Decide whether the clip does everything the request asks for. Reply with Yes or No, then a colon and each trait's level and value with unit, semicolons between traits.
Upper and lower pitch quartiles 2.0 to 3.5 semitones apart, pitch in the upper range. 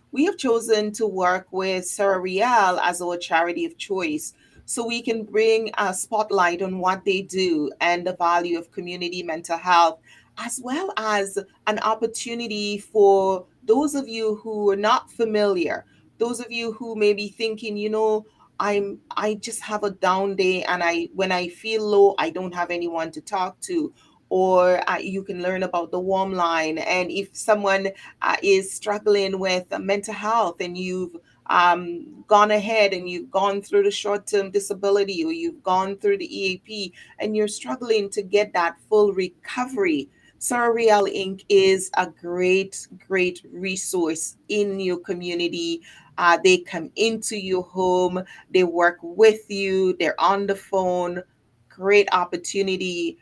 Yes: average, 3.0 semitones; high, 195 Hz